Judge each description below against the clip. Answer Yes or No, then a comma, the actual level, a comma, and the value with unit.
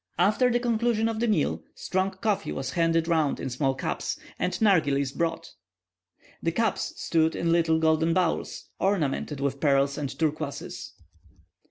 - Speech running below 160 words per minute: Yes, average, 150 wpm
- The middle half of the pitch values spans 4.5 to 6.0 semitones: Yes, average, 5.2 semitones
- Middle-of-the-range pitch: Yes, medium, 165 Hz